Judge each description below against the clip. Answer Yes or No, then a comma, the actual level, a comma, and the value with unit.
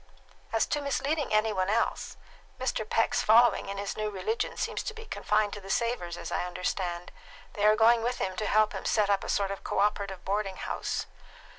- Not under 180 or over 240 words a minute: Yes, average, 200 wpm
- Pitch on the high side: Yes, high, 210 Hz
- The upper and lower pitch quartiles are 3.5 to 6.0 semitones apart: No, average, 3.0 semitones